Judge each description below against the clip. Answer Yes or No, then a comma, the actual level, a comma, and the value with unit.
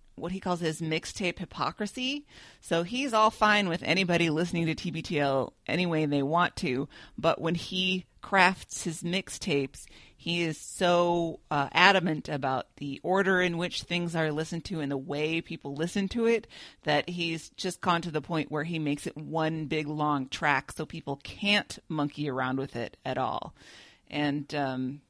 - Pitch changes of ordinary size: Yes, average, 3.4 semitones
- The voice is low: No, medium, 165 Hz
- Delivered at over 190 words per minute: No, average, 175 wpm